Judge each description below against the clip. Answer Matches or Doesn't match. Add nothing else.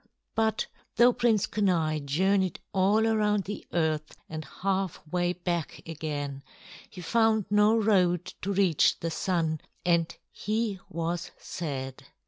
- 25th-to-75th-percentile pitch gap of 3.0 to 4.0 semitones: Doesn't match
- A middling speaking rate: Doesn't match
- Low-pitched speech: Doesn't match